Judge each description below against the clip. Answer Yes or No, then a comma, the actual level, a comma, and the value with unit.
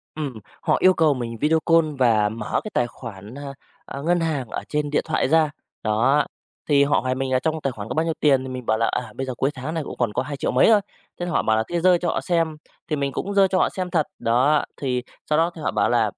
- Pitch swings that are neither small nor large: Yes, average, 4.5 semitones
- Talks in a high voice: No, medium, 145 Hz